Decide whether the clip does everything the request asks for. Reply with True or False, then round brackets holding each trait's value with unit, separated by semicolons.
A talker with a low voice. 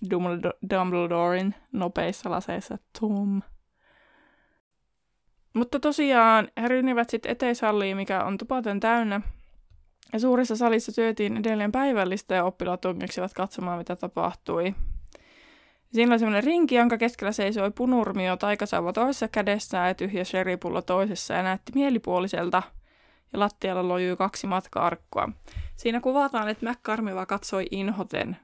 False (205 Hz)